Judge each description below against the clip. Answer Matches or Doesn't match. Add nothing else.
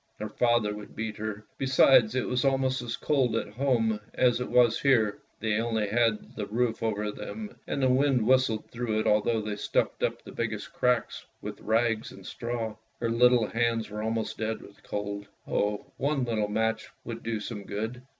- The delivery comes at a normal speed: Matches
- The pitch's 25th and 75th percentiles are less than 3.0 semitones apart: Matches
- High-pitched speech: Doesn't match